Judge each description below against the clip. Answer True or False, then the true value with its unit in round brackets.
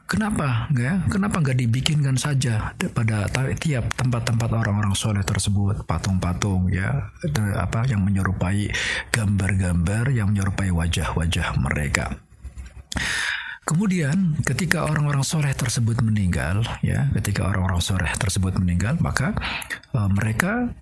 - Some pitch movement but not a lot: False (6.0 semitones)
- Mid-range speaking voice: False (110 Hz)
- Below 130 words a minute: True (110 wpm)